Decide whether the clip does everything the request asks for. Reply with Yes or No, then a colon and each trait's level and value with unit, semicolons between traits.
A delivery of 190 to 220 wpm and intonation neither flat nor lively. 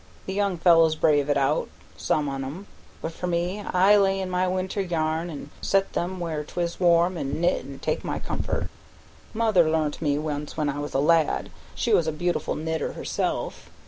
Yes: average, 195 wpm; average, 3.4 semitones